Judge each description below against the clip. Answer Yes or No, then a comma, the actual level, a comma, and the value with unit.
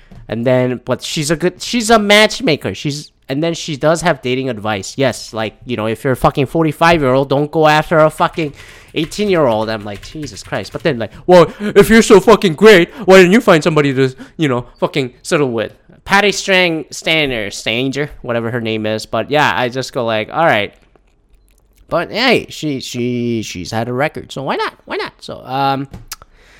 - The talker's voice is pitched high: No, medium, 140 Hz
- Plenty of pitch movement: Yes, wide, 5.7 semitones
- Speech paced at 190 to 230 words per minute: Yes, fast, 205 wpm